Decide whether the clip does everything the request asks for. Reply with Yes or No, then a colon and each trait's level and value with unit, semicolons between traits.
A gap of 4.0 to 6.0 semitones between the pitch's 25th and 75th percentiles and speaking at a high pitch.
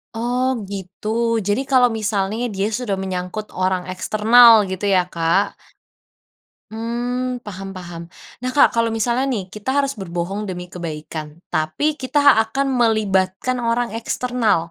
Yes: average, 4.6 semitones; high, 210 Hz